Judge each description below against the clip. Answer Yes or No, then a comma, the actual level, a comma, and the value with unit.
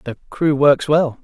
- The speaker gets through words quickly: No, average, 195 wpm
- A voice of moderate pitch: Yes, medium, 145 Hz